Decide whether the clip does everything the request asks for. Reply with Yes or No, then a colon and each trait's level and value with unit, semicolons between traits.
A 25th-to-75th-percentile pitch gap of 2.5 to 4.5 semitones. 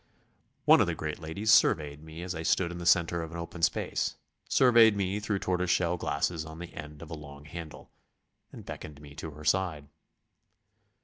Yes: average, 2.9 semitones